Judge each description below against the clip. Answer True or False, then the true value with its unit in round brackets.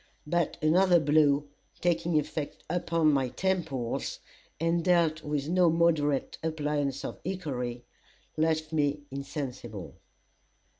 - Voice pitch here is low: False (155 Hz)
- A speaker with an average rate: False (105 wpm)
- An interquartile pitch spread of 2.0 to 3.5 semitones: True (2.9 semitones)